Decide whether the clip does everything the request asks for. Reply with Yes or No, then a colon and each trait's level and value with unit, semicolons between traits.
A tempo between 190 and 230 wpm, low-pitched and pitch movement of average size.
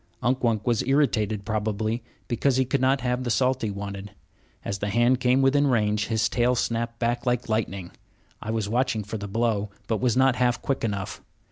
Yes: average, 200 wpm; low, 115 Hz; average, 3.0 semitones